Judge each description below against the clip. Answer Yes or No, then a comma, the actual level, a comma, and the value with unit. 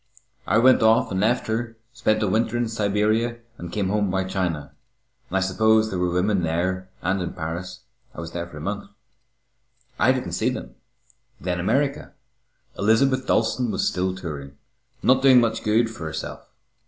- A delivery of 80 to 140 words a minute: No, average, 170 wpm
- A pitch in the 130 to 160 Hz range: No, low, 100 Hz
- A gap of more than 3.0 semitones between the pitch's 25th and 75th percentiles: Yes, average, 3.8 semitones